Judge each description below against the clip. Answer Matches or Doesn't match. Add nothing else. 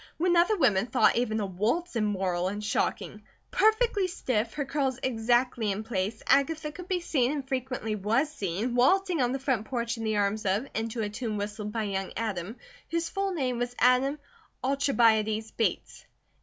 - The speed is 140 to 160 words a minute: Doesn't match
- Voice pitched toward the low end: Doesn't match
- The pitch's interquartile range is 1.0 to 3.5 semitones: Doesn't match